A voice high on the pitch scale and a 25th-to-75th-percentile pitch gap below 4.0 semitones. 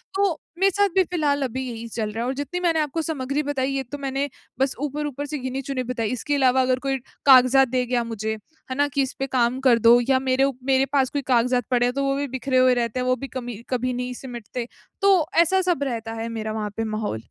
Yes: very high, 260 Hz; narrow, 2.6 semitones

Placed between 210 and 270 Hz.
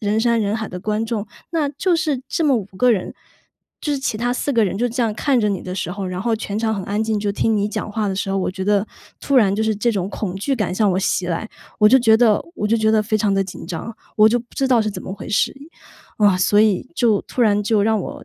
Yes: high, 215 Hz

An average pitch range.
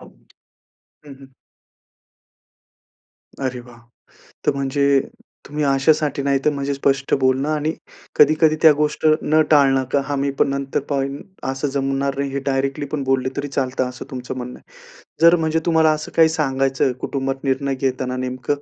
No: narrow, 1.9 semitones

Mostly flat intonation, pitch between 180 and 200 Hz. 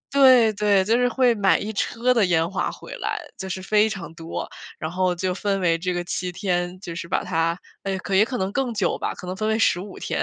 No: average, 3.5 semitones; high, 190 Hz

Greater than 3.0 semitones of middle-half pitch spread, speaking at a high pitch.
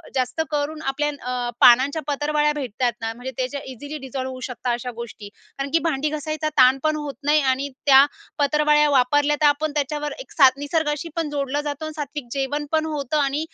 No: narrow, 2.4 semitones; very high, 285 Hz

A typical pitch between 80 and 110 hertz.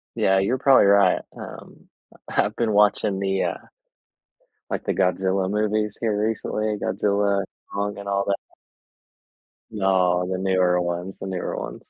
Yes: low, 100 Hz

